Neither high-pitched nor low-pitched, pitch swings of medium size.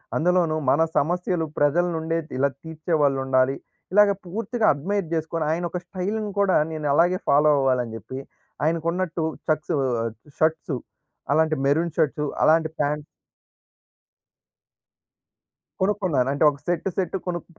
Yes: medium, 160 Hz; average, 3.5 semitones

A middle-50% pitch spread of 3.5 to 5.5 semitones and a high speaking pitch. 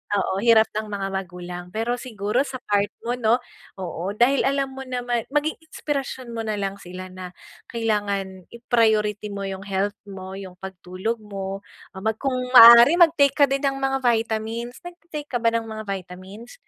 Yes: average, 4.2 semitones; high, 220 Hz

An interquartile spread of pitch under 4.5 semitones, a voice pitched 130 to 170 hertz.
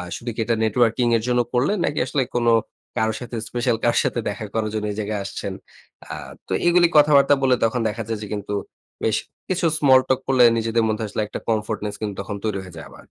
No: average, 2.9 semitones; low, 115 Hz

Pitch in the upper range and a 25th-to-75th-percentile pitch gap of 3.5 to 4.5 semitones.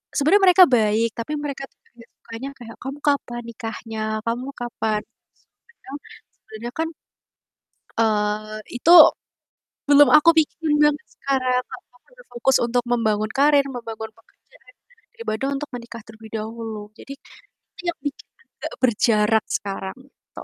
Yes: high, 240 Hz; average, 4.1 semitones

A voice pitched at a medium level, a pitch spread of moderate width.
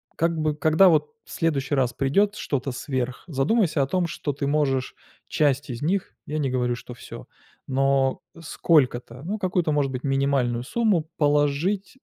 Yes: medium, 145 Hz; average, 3.7 semitones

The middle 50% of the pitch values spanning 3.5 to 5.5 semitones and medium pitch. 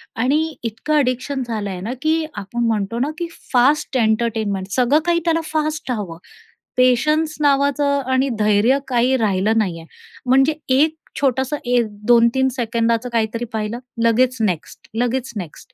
No: average, 4.2 semitones; high, 245 Hz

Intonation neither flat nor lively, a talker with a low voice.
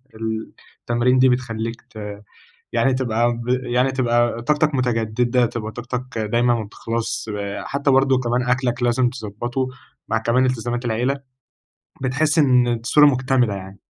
No: narrow, 2.1 semitones; low, 120 Hz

